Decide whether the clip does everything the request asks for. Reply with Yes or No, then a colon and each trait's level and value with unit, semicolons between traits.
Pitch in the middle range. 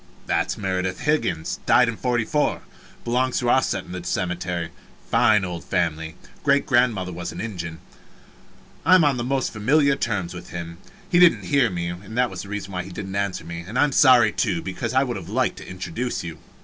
No: low, 105 Hz